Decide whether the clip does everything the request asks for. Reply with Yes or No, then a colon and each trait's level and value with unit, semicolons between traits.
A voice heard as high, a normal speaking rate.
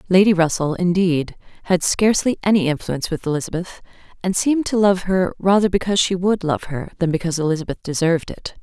No: medium, 180 Hz; average, 175 wpm